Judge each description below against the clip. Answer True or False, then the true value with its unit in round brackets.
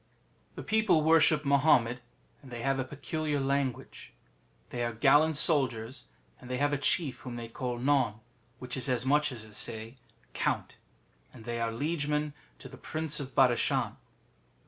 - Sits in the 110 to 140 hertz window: True (135 Hz)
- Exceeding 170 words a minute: False (165 wpm)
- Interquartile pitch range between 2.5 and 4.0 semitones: True (3.6 semitones)